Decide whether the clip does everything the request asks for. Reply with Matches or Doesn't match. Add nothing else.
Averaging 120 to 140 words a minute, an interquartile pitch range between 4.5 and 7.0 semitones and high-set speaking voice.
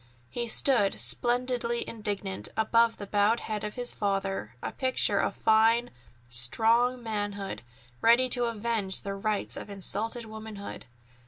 Doesn't match